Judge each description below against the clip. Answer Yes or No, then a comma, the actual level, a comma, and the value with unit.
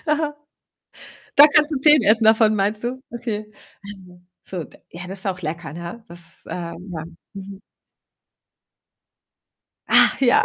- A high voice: Yes, high, 205 Hz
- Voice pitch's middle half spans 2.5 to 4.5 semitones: No, average, 5.2 semitones